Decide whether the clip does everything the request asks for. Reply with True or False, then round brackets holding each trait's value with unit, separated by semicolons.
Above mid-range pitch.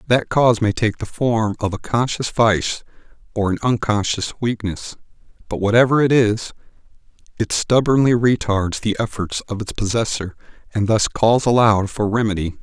False (110 Hz)